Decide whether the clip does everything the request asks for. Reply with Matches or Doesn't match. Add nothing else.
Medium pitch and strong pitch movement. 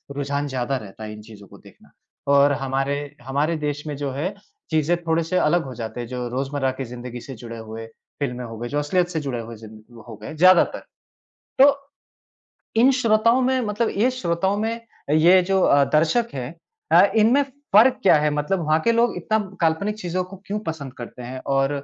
Matches